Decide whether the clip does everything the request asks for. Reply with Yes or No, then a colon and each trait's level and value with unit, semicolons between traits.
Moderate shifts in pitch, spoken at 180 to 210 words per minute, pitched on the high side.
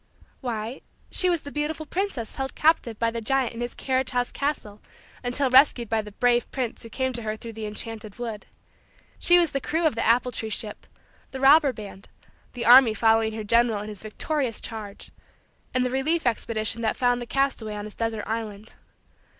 Yes: average, 3.5 semitones; average, 195 wpm; high, 235 Hz